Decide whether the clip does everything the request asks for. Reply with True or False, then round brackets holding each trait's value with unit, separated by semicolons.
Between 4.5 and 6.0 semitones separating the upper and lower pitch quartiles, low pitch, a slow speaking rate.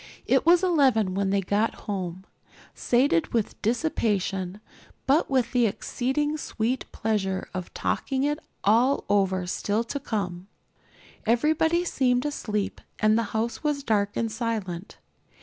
False (5.2 semitones; 225 Hz; 130 wpm)